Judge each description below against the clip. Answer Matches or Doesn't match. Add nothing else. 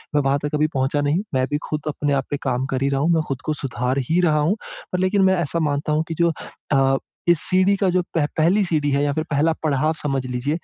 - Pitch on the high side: Doesn't match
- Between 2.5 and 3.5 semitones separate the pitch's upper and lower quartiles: Matches